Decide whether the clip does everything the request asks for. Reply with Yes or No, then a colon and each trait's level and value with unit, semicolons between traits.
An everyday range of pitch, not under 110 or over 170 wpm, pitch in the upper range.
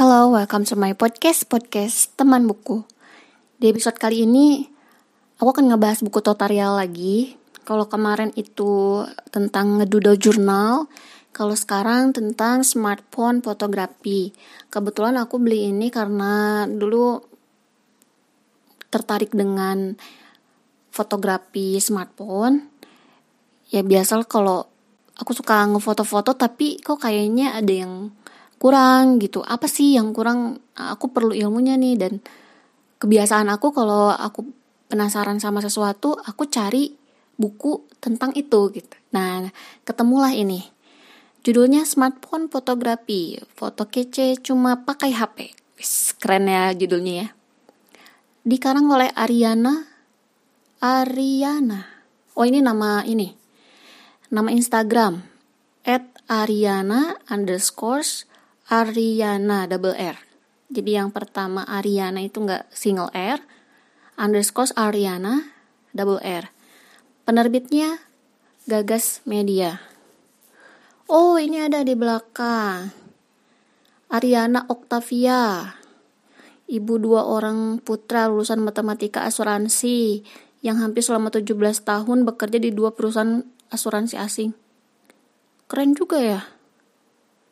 No: average, 3.6 semitones; average, 100 wpm; high, 230 Hz